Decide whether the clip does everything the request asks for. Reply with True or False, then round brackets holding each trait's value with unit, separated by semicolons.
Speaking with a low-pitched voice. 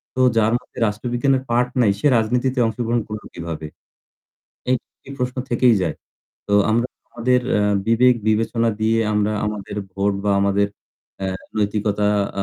True (110 Hz)